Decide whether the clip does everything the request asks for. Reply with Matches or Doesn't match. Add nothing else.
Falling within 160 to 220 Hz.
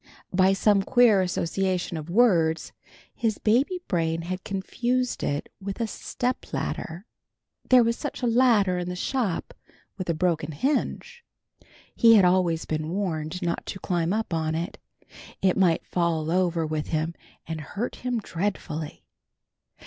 Matches